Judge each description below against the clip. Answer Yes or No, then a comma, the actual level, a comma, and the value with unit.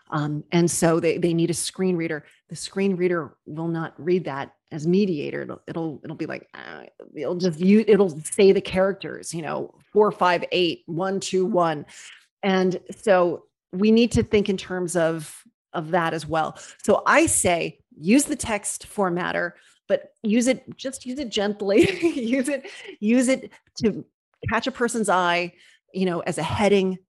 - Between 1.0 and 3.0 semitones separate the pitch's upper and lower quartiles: No, average, 4.0 semitones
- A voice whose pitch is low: No, medium, 185 Hz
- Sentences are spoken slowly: No, average, 170 wpm